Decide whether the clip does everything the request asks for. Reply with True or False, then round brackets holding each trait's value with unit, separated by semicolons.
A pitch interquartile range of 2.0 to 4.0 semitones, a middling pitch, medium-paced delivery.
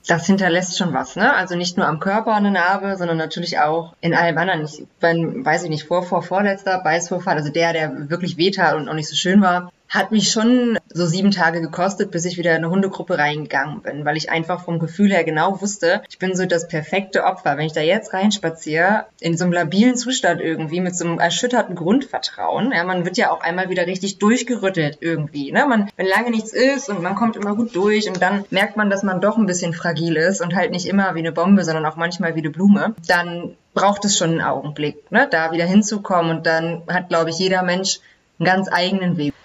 False (3.1 semitones; 180 Hz; 230 wpm)